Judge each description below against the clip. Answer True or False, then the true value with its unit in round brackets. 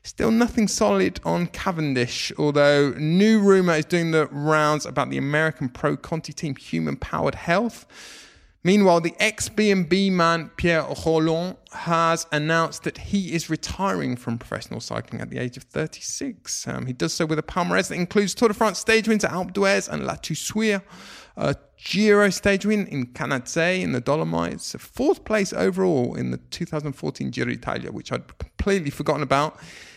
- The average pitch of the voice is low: False (165 Hz)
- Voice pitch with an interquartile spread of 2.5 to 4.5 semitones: False (5.3 semitones)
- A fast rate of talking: False (165 wpm)